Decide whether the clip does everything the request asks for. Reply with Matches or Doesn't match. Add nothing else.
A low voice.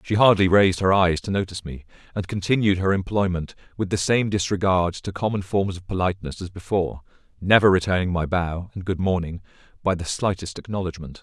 Matches